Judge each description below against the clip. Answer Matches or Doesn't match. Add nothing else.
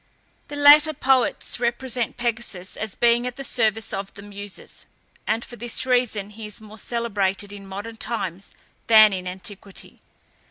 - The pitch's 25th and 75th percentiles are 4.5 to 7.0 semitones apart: Doesn't match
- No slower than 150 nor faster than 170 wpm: Matches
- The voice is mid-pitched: Doesn't match